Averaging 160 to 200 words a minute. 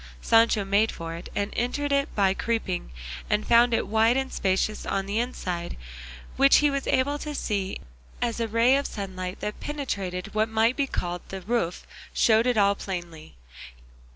Yes: average, 175 wpm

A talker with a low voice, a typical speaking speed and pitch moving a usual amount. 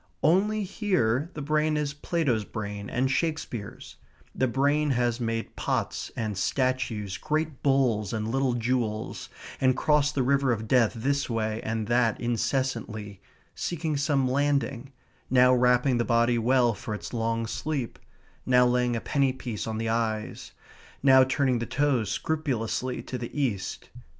Yes: low, 125 Hz; average, 150 wpm; average, 3.6 semitones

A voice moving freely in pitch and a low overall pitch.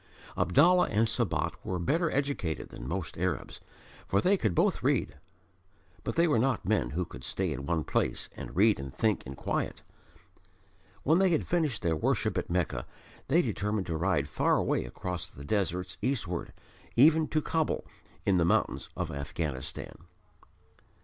Yes: wide, 8.7 semitones; very low, 95 Hz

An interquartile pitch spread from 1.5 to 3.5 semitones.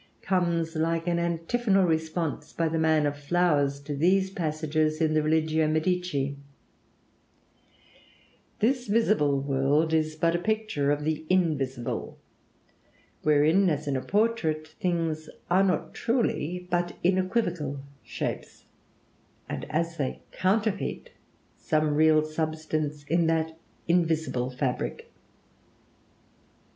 Yes: average, 2.8 semitones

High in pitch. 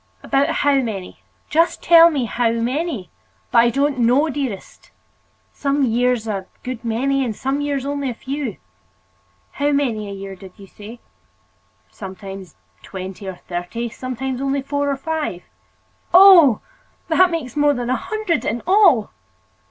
Yes: very high, 255 Hz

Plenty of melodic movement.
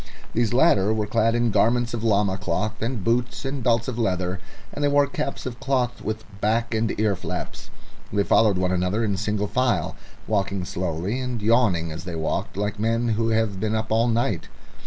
No: average, 3.2 semitones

